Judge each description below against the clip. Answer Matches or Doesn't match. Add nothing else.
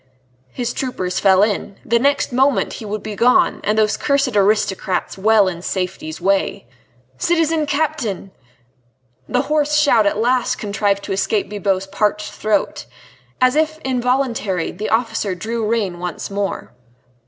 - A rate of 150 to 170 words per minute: Doesn't match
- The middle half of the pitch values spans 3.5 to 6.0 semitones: Matches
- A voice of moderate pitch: Doesn't match